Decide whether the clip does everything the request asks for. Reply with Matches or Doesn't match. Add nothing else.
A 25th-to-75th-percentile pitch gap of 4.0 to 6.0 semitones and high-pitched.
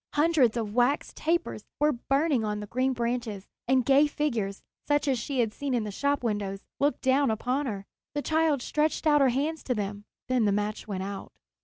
Matches